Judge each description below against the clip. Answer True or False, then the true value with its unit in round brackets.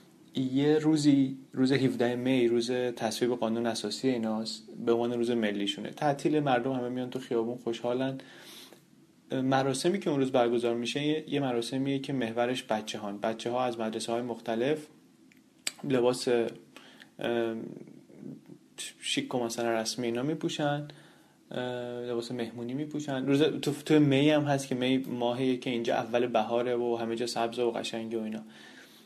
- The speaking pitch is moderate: False (125 Hz)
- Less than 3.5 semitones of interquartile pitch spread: True (2.5 semitones)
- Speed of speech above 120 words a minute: True (145 wpm)